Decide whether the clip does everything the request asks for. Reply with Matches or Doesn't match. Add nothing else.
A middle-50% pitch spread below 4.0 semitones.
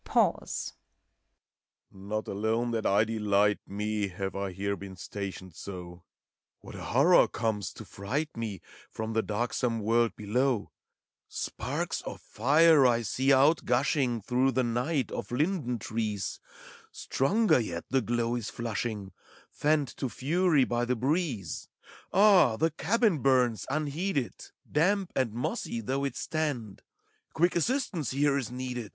Doesn't match